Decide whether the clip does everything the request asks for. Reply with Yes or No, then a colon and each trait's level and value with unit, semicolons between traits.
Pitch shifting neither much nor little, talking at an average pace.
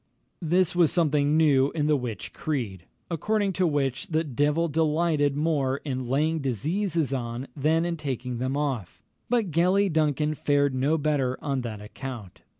Yes: average, 3.7 semitones; average, 155 wpm